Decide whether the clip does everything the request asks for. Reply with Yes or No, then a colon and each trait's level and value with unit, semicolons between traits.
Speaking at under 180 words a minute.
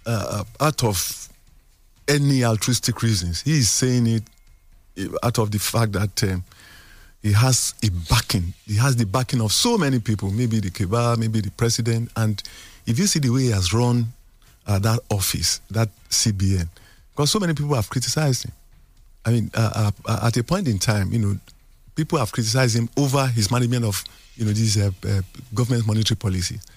No: average, 185 wpm